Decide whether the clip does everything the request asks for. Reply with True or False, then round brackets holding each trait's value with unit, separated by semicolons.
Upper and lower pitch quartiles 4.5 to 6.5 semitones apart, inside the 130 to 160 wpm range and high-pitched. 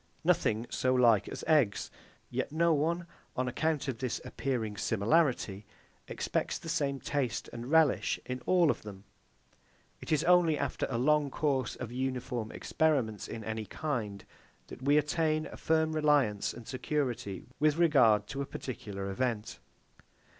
False (5.2 semitones; 150 wpm; 130 Hz)